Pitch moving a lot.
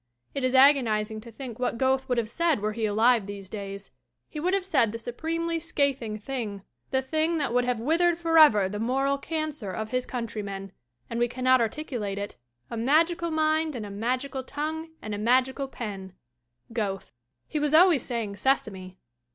Yes: wide, 5.8 semitones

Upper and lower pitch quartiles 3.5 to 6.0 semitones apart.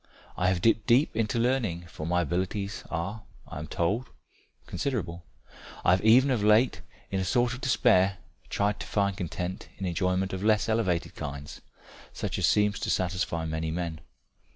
Yes: average, 4.1 semitones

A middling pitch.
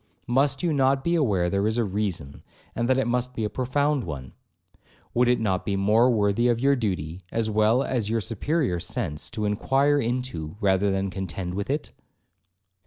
No: low, 110 Hz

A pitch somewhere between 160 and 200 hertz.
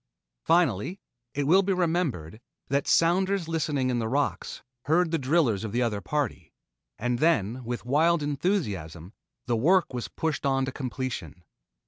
No: medium, 140 Hz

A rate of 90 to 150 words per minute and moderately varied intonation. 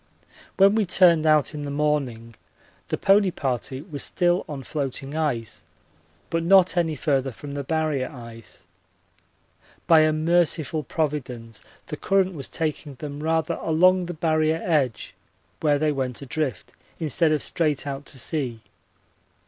Yes: average, 145 wpm; average, 3.2 semitones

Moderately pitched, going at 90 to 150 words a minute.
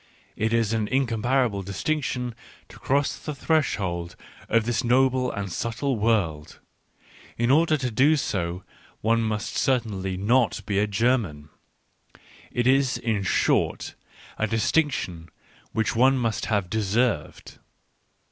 No: low, 115 Hz; slow, 135 wpm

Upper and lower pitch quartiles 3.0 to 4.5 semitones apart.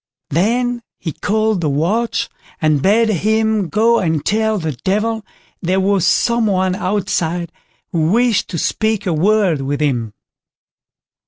No: average, 5.0 semitones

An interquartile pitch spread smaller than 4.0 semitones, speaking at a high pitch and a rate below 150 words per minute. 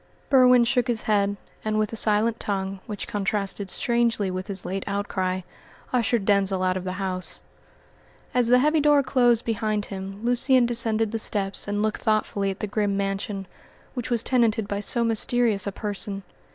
No: average, 3.1 semitones; high, 210 Hz; average, 175 wpm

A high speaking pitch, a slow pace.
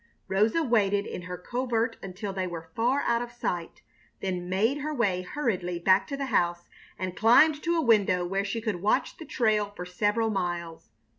No: high, 205 Hz; average, 190 wpm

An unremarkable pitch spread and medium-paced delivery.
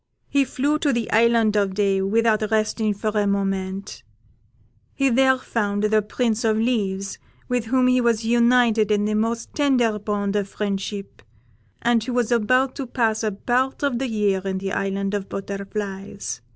Yes: average, 3.1 semitones; average, 170 wpm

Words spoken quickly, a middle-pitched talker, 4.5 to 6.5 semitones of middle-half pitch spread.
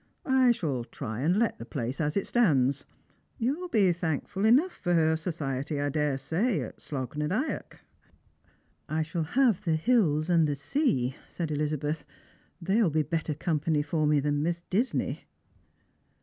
No: average, 165 wpm; medium, 160 Hz; average, 5.1 semitones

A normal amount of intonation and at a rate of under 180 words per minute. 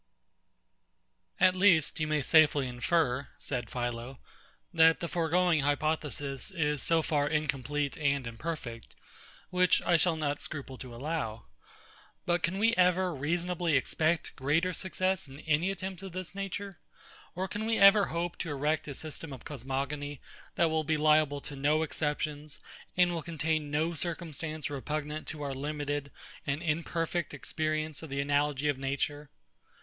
Yes: average, 3.0 semitones; average, 150 wpm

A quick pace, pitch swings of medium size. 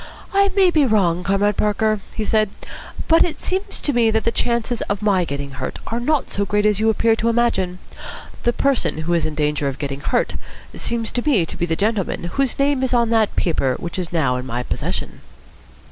No: fast, 215 wpm; wide, 5.8 semitones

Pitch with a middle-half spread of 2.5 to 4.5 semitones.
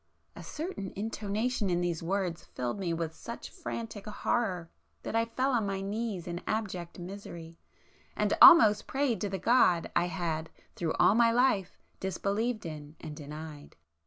No: average, 4.9 semitones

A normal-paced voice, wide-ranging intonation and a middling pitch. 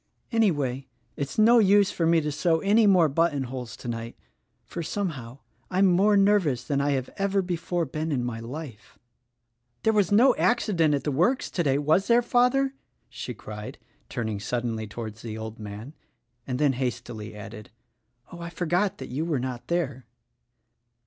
Yes: average, 170 wpm; wide, 7.5 semitones; medium, 145 Hz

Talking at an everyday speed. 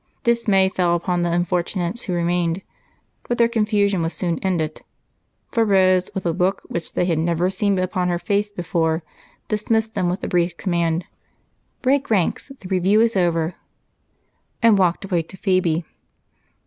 Yes: average, 160 wpm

